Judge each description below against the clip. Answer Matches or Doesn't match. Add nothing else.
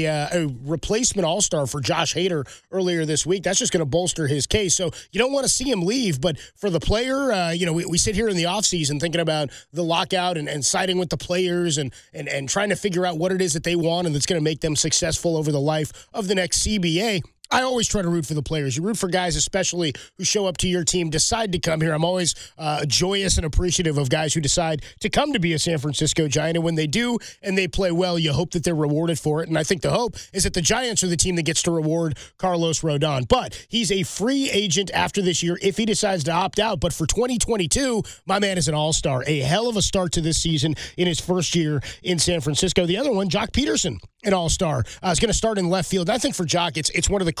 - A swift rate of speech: Matches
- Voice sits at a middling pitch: Matches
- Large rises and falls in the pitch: Doesn't match